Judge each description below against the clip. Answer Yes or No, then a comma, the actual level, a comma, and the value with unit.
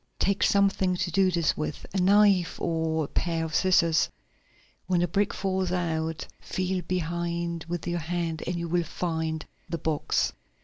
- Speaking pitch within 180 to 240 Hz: No, medium, 170 Hz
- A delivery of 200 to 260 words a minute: No, average, 165 wpm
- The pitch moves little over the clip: Yes, narrow, 2.2 semitones